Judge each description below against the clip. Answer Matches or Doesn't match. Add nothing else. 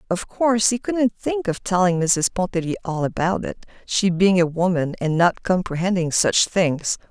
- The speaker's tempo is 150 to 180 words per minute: Matches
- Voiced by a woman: Matches